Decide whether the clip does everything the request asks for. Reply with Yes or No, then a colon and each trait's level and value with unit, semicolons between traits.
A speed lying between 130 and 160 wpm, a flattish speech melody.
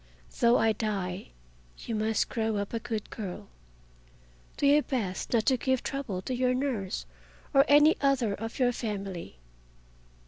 No: average, 150 wpm; average, 4.4 semitones